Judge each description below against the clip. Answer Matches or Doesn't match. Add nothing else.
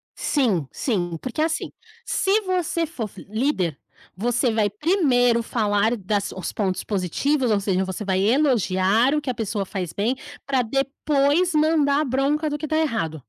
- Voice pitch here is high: Matches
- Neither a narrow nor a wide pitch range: Doesn't match